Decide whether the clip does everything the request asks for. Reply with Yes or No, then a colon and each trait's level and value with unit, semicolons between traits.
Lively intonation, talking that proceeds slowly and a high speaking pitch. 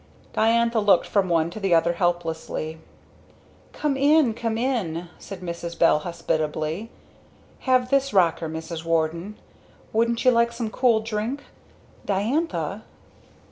Yes: wide, 5.8 semitones; slow, 125 wpm; high, 200 Hz